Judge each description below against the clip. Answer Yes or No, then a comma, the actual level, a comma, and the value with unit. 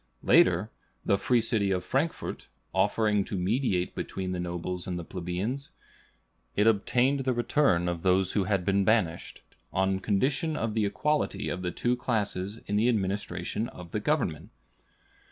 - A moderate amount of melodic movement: Yes, average, 4.6 semitones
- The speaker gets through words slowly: No, average, 155 wpm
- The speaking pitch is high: No, low, 100 Hz